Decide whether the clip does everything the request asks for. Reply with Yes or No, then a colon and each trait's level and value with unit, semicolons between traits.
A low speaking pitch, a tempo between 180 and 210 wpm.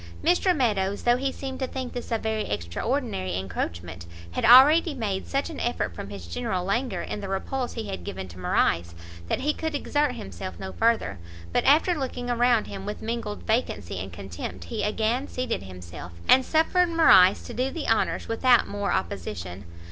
No: high, 220 Hz; average, 185 wpm